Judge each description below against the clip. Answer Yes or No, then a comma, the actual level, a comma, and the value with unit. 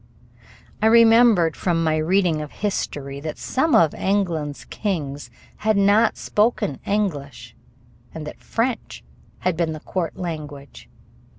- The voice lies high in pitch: No, medium, 170 Hz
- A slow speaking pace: Yes, slow, 125 wpm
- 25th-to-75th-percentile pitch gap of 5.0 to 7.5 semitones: Yes, wide, 5.5 semitones